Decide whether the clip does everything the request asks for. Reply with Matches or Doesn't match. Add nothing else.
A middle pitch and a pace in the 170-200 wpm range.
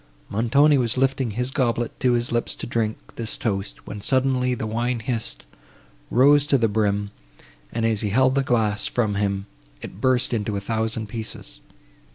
Doesn't match